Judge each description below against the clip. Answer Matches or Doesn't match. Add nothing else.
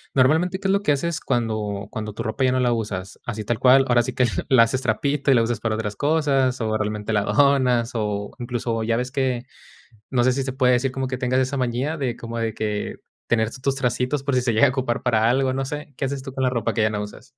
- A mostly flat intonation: Doesn't match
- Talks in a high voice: Doesn't match